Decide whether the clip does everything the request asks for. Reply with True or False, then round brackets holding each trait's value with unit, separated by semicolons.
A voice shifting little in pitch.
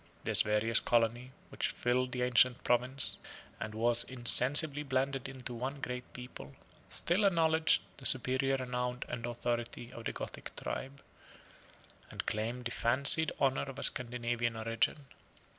True (2.2 semitones)